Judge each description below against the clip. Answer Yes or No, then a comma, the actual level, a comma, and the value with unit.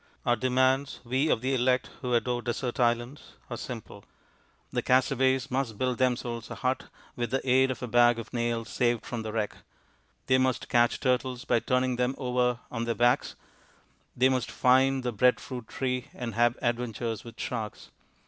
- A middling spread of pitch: No, narrow, 1.5 semitones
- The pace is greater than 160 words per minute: Yes, average, 175 wpm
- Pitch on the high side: No, low, 125 Hz